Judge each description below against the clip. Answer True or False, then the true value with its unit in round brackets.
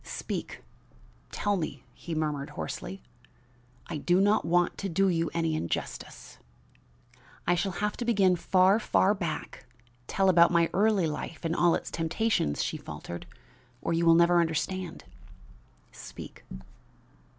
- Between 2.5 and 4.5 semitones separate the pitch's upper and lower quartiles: True (2.9 semitones)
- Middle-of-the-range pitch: True (175 Hz)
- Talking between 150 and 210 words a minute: False (140 wpm)